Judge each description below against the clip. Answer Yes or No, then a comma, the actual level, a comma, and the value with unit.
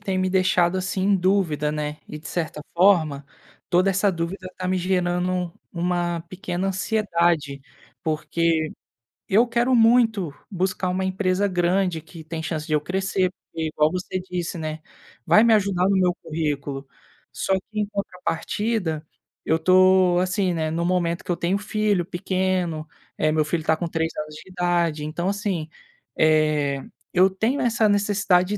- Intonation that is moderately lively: Yes, average, 3.0 semitones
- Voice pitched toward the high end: No, medium, 180 Hz